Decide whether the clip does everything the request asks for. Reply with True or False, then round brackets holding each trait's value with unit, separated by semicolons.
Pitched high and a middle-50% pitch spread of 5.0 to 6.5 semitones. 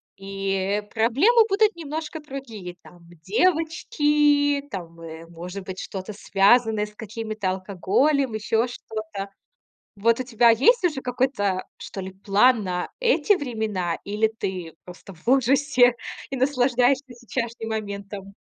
True (225 Hz; 5.6 semitones)